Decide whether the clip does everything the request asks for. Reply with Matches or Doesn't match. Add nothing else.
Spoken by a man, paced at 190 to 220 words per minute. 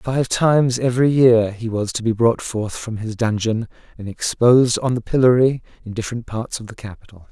Matches